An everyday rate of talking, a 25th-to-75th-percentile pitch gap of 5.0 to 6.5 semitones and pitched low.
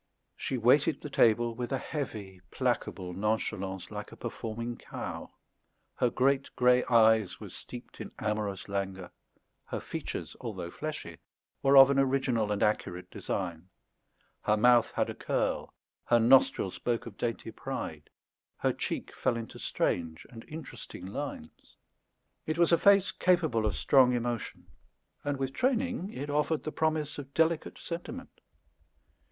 Yes: average, 145 wpm; wide, 5.4 semitones; low, 120 Hz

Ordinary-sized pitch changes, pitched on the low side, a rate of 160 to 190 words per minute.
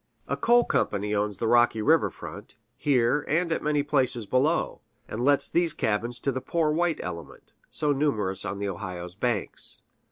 No: wide, 6.4 semitones; low, 120 Hz; average, 170 wpm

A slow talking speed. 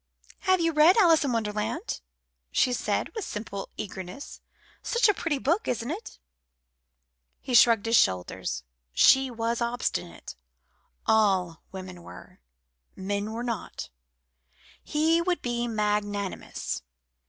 Yes: slow, 120 wpm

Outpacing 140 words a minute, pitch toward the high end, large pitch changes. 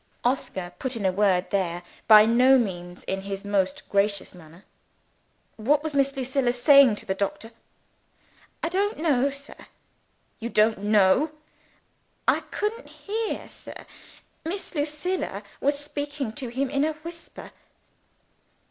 No: slow, 135 wpm; very high, 250 Hz; wide, 6.7 semitones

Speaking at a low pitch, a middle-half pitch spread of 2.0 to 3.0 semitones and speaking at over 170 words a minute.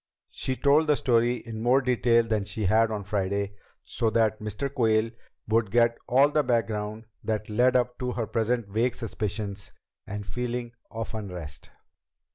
No: low, 115 Hz; narrow, 2.6 semitones; average, 160 wpm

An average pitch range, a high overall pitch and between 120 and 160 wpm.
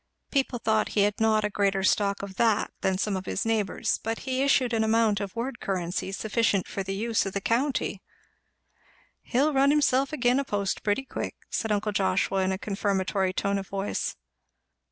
No: average, 3.2 semitones; high, 210 Hz; average, 190 wpm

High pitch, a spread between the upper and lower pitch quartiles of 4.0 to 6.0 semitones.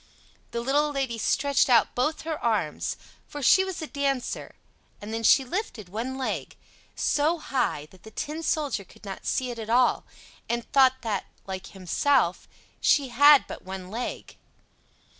Yes: very high, 250 Hz; average, 4.8 semitones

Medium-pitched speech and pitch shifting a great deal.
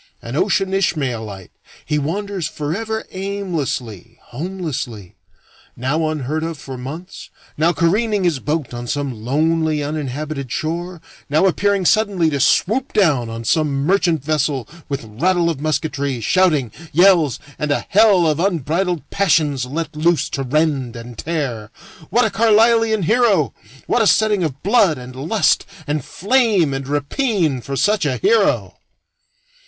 Yes: medium, 155 Hz; wide, 5.8 semitones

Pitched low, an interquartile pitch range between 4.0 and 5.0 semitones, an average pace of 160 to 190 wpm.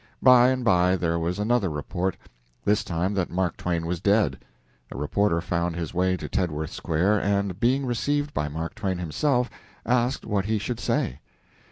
Yes: very low, 95 Hz; average, 4.7 semitones; average, 175 wpm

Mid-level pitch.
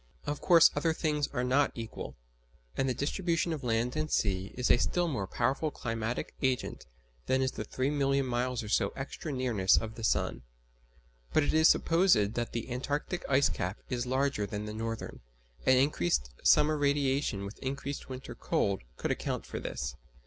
No: low, 130 Hz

